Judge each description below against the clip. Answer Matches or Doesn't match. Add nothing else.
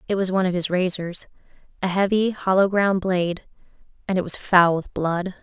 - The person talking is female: Matches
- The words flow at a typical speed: Matches